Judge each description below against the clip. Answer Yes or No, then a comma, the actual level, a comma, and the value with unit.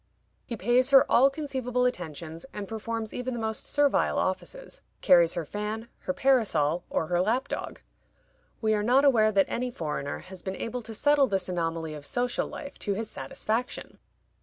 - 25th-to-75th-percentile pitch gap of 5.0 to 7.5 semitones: Yes, wide, 5.6 semitones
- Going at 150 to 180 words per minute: Yes, average, 170 wpm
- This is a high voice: Yes, high, 220 Hz